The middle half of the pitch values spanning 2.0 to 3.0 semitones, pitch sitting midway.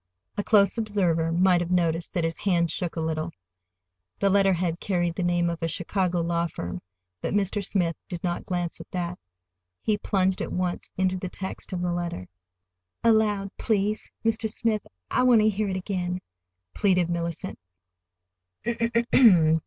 Yes: average, 2.7 semitones; medium, 180 Hz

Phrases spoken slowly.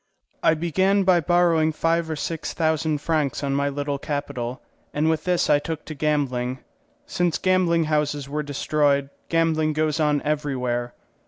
No: average, 155 wpm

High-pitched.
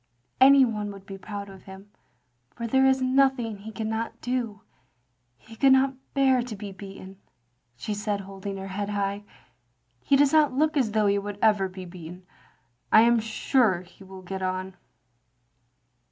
Yes: high, 205 Hz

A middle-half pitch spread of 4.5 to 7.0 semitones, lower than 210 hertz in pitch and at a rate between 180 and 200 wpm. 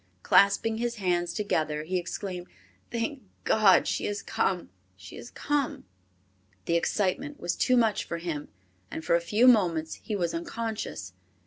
No: average, 5.0 semitones; high, 190 Hz; average, 150 wpm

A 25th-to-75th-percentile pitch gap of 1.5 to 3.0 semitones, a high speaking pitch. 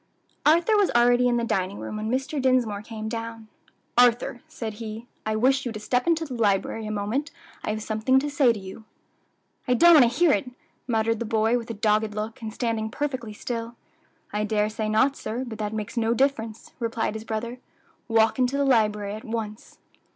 Yes: narrow, 2.4 semitones; high, 225 Hz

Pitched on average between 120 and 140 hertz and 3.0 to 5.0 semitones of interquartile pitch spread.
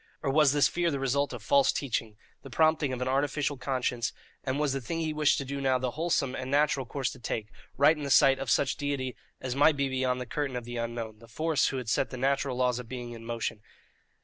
No: low, 135 Hz; narrow, 2.6 semitones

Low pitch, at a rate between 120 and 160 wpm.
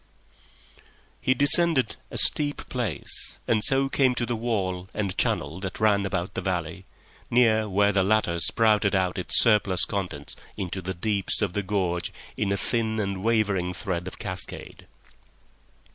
Yes: low, 100 Hz; average, 155 wpm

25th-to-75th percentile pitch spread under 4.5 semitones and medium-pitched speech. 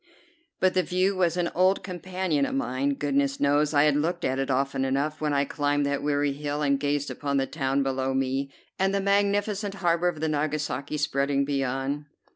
Yes: average, 4.0 semitones; medium, 145 Hz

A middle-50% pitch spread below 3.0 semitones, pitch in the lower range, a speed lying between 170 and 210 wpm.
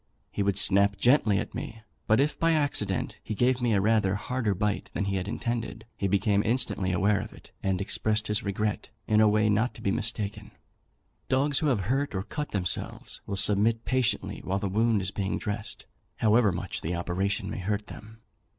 Yes: narrow, 2.6 semitones; low, 105 Hz; average, 195 wpm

